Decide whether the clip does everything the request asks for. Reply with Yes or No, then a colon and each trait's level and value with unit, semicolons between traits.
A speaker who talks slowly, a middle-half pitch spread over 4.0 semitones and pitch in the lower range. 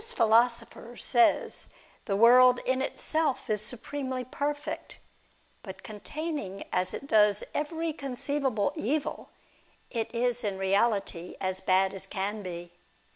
No: slow, 120 wpm; average, 5.1 semitones; high, 235 Hz